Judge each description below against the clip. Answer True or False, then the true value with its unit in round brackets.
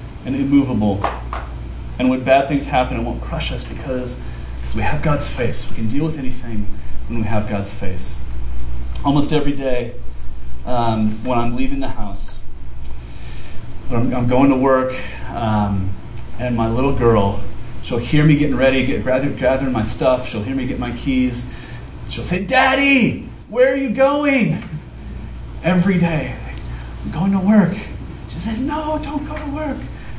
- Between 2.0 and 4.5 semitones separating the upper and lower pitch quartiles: False (5.2 semitones)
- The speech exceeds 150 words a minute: True (165 wpm)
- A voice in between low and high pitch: False (125 Hz)